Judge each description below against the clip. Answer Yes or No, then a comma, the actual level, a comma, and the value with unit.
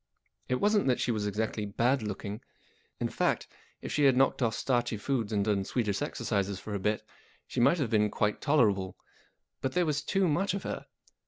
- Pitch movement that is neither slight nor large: Yes, average, 4.9 semitones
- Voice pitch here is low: Yes, low, 115 Hz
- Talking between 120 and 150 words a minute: No, average, 195 wpm